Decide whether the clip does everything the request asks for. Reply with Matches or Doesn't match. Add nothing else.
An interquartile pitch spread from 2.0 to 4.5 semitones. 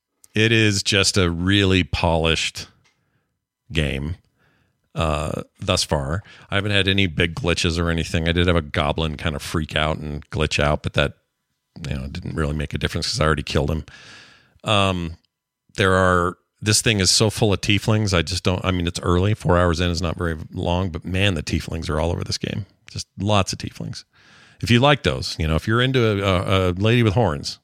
Matches